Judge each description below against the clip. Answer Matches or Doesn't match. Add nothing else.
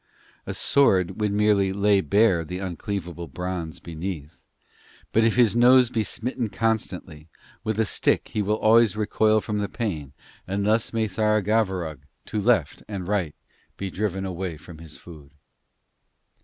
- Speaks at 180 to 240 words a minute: Doesn't match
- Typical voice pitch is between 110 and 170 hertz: Doesn't match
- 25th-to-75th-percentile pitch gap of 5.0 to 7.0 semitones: Doesn't match